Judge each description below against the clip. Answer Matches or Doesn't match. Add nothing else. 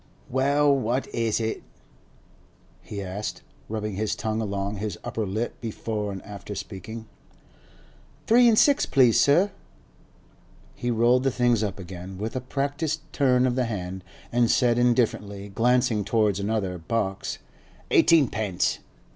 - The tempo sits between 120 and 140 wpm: Matches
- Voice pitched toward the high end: Doesn't match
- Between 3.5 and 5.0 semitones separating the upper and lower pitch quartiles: Matches